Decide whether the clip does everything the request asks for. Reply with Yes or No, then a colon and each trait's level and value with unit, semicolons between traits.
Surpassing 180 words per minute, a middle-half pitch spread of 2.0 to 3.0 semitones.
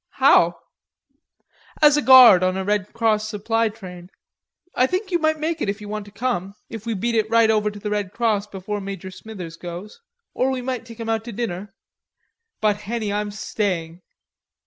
Yes: average, 190 wpm; average, 2.7 semitones